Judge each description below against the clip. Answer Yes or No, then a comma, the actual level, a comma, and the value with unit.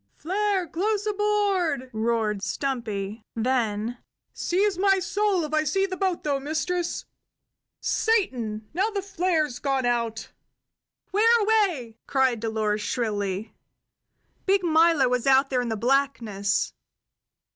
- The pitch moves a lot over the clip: Yes, wide, 8.7 semitones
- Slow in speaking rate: Yes, slow, 115 wpm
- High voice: Yes, very high, 280 Hz